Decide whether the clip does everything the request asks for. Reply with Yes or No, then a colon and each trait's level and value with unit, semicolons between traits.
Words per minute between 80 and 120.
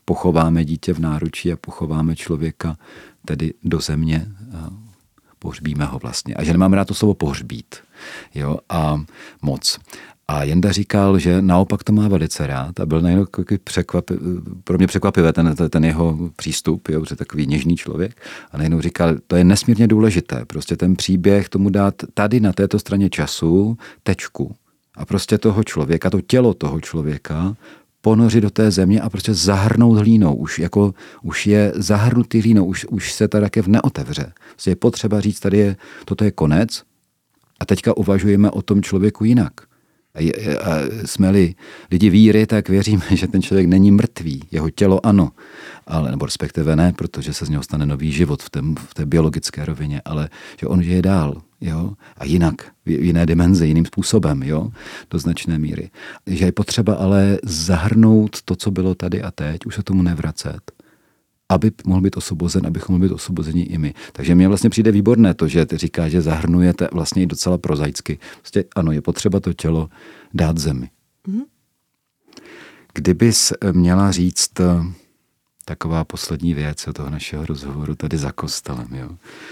No: fast, 170 wpm